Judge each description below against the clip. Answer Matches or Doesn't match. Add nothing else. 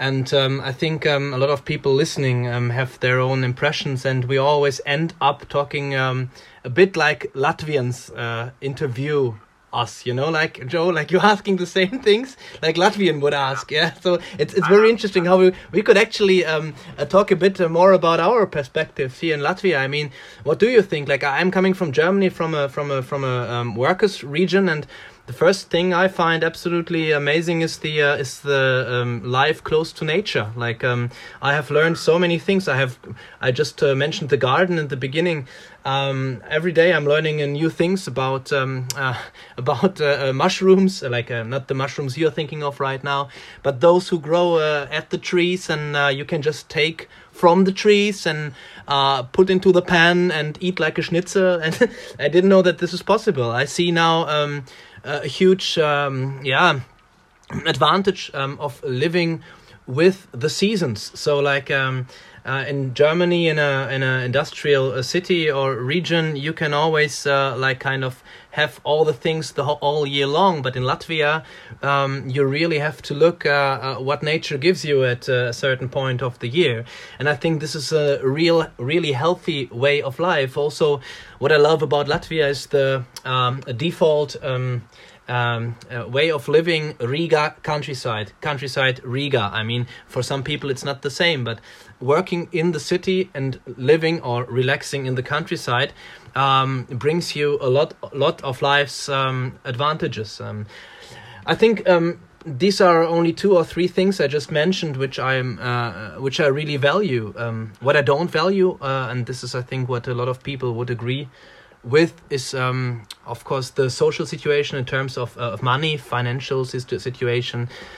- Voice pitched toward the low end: Doesn't match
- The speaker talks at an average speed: Matches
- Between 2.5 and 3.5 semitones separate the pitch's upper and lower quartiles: Doesn't match